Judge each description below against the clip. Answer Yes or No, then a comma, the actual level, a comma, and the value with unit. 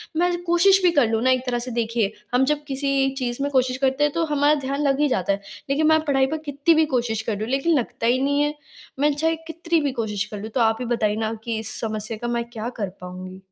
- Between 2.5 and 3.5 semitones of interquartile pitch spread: No, average, 4.7 semitones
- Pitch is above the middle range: Yes, very high, 260 Hz